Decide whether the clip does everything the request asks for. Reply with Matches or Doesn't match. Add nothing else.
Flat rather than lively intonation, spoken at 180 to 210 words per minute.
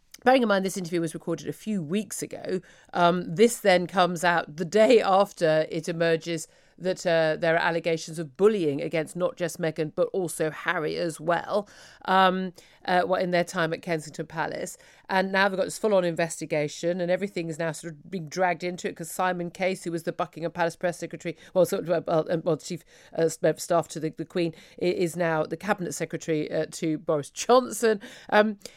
Matches